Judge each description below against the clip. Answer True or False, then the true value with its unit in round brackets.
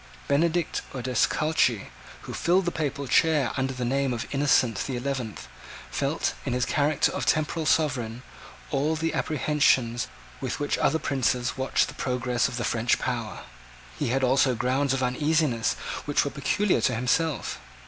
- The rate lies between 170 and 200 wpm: False (155 wpm)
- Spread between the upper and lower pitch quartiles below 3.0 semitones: False (3.3 semitones)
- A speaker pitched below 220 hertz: True (135 Hz)